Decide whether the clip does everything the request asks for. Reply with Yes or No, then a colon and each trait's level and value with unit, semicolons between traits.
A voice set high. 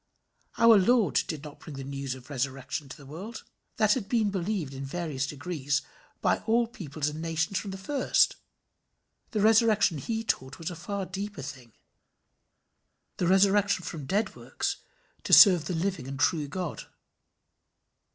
No: medium, 175 Hz